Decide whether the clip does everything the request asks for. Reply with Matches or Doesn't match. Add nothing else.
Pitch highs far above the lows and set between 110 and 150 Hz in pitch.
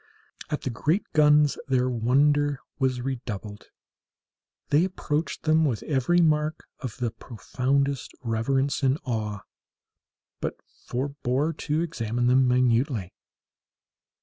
Doesn't match